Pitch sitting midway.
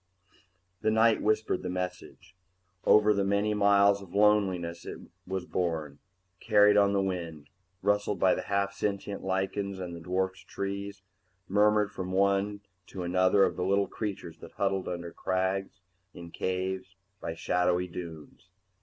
No: very low, 95 Hz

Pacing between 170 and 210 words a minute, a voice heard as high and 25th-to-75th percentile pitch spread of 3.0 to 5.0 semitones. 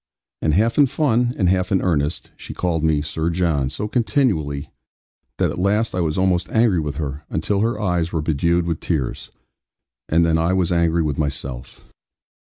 No: average, 185 wpm; very low, 85 Hz; average, 4.2 semitones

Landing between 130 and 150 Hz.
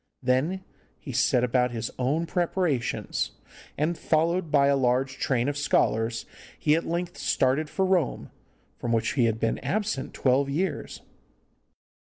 Yes: medium, 140 Hz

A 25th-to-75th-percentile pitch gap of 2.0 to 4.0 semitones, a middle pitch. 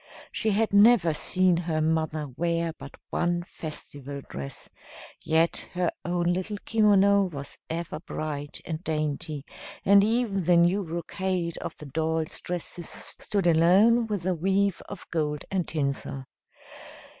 Yes: average, 3.6 semitones; medium, 170 Hz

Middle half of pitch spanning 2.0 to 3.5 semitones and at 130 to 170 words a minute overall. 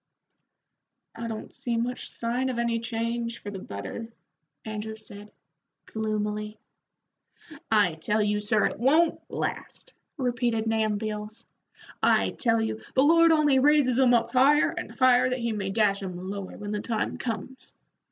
Yes: average, 3.1 semitones; average, 150 wpm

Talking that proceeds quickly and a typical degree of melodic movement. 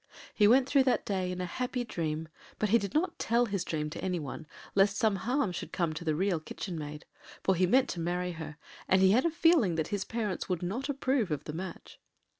No: fast, 235 wpm; wide, 5.8 semitones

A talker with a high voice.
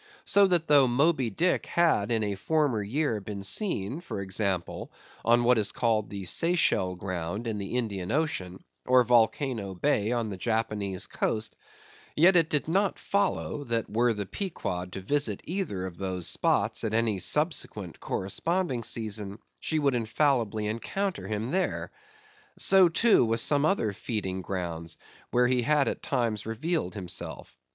No: low, 115 Hz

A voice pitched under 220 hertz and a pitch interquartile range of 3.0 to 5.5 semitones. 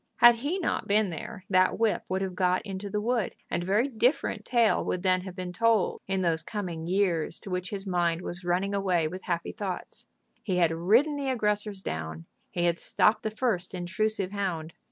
Yes: high, 190 Hz; average, 3.3 semitones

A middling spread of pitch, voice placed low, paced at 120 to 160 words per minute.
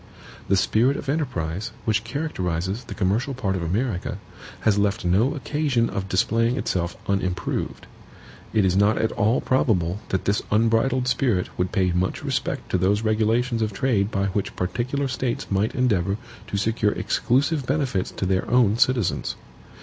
Yes: average, 4.6 semitones; low, 110 Hz; average, 155 wpm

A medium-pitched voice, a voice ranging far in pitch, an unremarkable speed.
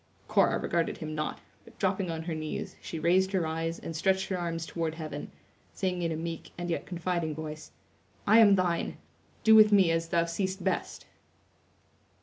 No: medium, 170 Hz; narrow, 2.6 semitones; average, 180 wpm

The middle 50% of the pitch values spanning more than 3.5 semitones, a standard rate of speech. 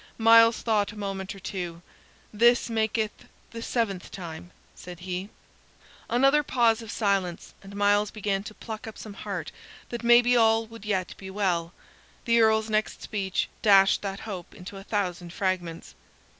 No: average, 2.9 semitones; average, 160 wpm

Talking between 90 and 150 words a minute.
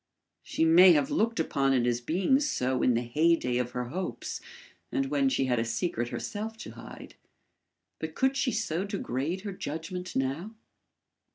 No: average, 170 wpm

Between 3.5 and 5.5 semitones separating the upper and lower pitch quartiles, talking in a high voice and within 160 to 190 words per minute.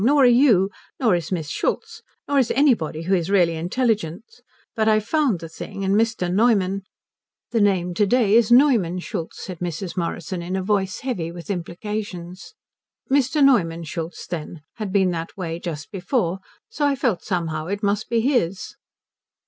Yes: average, 5.0 semitones; high, 195 Hz; average, 180 wpm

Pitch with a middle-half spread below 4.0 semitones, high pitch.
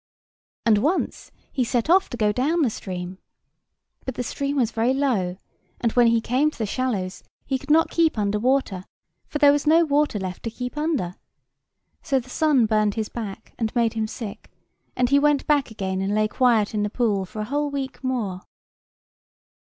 No: average, 5.0 semitones; high, 240 Hz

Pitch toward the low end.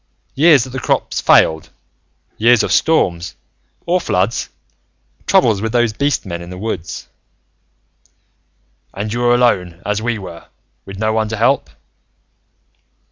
Yes: low, 110 Hz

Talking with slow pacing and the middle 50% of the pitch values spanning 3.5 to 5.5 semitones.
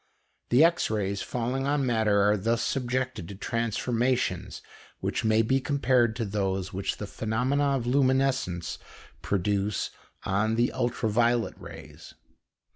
Yes: slow, 130 wpm; average, 3.8 semitones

